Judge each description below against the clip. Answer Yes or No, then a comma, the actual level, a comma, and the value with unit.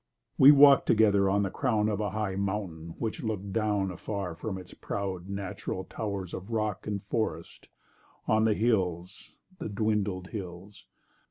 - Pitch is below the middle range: Yes, low, 100 Hz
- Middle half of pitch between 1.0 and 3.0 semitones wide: Yes, narrow, 2.4 semitones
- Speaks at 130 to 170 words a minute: Yes, average, 155 wpm